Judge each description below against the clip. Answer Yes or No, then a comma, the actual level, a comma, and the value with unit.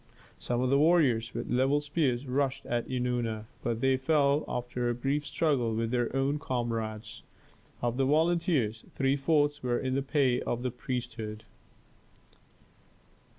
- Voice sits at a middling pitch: No, low, 130 Hz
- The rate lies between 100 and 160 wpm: Yes, average, 150 wpm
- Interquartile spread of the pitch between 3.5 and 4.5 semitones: No, average, 2.9 semitones